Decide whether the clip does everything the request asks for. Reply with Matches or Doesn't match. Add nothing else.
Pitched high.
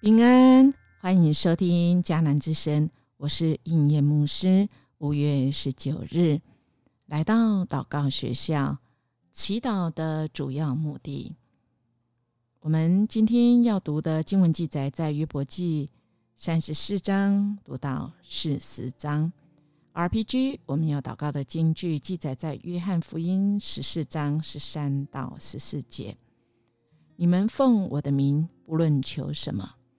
Doesn't match